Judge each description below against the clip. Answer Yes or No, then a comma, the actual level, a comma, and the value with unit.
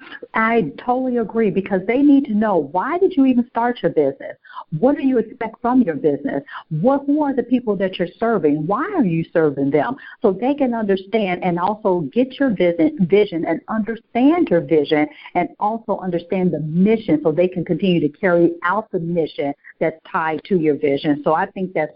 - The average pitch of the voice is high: Yes, high, 195 Hz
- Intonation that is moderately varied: No, wide, 6.1 semitones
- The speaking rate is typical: Yes, average, 195 wpm